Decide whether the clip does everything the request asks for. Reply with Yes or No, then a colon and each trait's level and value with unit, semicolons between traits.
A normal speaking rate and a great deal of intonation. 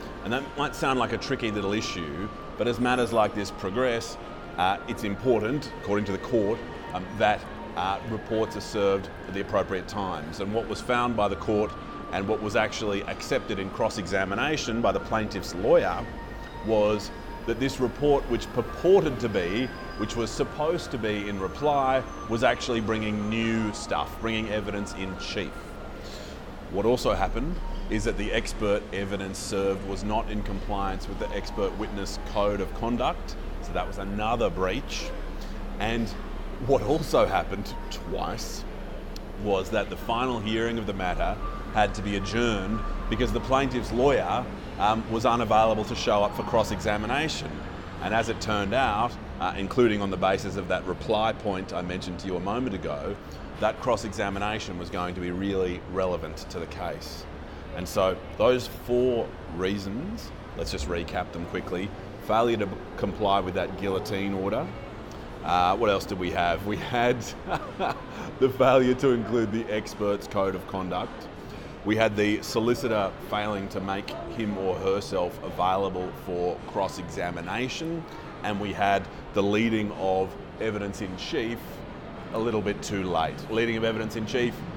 No: average, 165 wpm; average, 3.1 semitones